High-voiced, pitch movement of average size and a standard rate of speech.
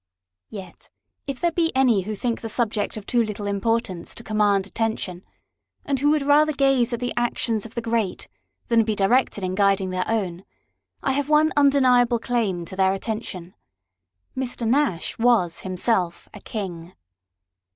Yes: high, 225 Hz; average, 4.4 semitones; average, 160 wpm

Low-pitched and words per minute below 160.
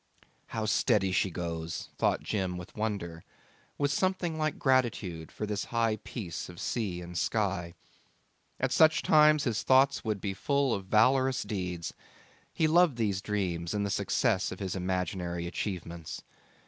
Yes: low, 100 Hz; average, 150 wpm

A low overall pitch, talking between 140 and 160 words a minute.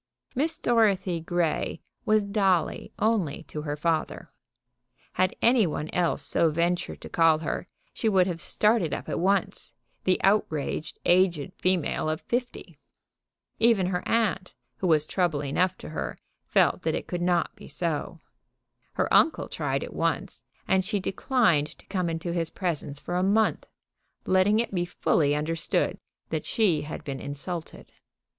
No: medium, 180 Hz; average, 155 wpm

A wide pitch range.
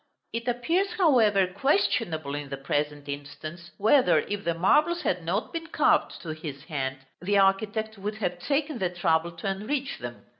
Yes: wide, 7.2 semitones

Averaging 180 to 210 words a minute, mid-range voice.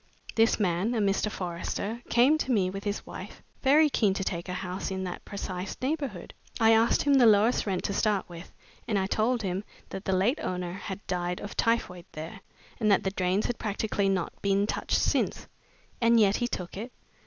No: average, 200 wpm; high, 200 Hz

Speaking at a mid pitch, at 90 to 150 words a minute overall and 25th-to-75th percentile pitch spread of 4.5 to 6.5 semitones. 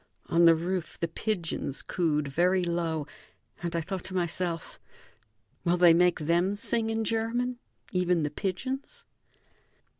No: medium, 180 Hz; average, 140 wpm; average, 3.2 semitones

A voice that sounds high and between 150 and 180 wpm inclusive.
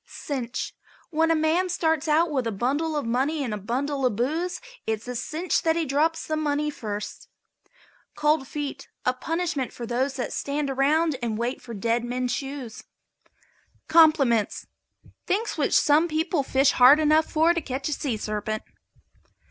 Yes: very high, 280 Hz; average, 165 wpm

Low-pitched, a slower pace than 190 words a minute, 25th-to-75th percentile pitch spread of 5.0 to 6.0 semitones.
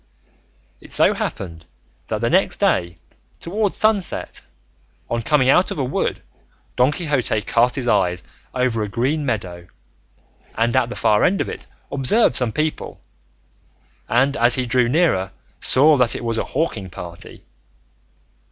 Yes: low, 125 Hz; average, 150 wpm; average, 5.3 semitones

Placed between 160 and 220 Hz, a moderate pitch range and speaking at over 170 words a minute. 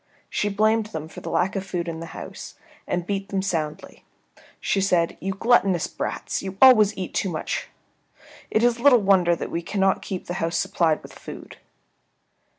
Yes: high, 190 Hz; average, 3.3 semitones; average, 180 wpm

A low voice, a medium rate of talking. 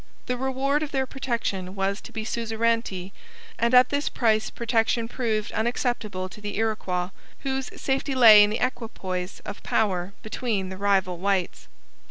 No: high, 220 Hz; average, 155 wpm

